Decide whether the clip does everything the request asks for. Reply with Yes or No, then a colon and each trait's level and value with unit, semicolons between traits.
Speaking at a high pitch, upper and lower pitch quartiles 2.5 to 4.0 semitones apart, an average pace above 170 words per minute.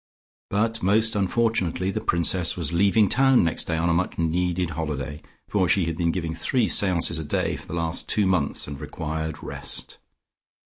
No: very low, 85 Hz; average, 3.5 semitones; average, 180 wpm